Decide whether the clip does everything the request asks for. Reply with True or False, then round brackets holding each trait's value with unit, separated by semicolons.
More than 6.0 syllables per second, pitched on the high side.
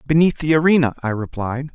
False (6.2 syllables/s; 140 Hz)